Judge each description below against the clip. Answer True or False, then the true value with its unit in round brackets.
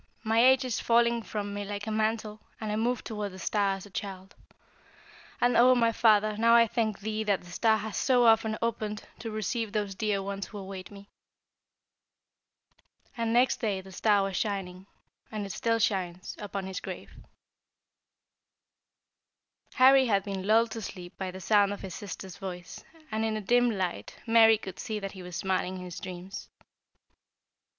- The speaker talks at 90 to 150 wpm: False (180 wpm)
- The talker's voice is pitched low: False (210 Hz)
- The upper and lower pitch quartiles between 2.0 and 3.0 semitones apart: True (2.7 semitones)